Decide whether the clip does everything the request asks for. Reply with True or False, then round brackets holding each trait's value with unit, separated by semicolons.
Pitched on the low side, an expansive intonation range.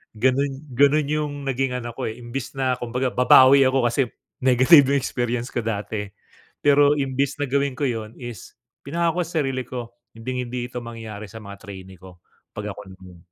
False (125 Hz; 3.3 semitones)